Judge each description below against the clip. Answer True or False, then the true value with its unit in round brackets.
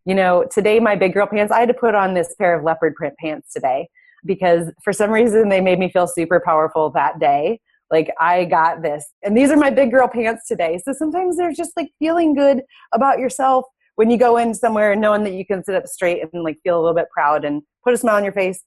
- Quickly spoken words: True (250 wpm)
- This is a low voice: False (205 Hz)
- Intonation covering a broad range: True (6.3 semitones)